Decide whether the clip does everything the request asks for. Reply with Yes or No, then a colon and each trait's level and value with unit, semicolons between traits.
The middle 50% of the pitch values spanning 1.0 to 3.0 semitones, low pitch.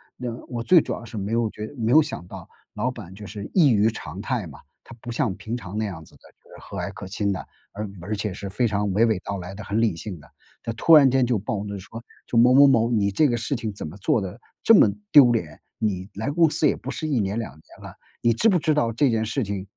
No: average, 3.5 semitones; low, 110 Hz